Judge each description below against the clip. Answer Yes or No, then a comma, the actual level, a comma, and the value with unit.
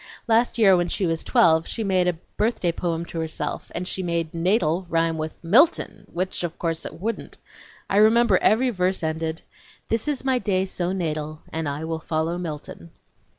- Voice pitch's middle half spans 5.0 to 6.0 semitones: No, average, 3.8 semitones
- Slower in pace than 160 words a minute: No, average, 185 wpm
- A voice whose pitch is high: No, medium, 175 Hz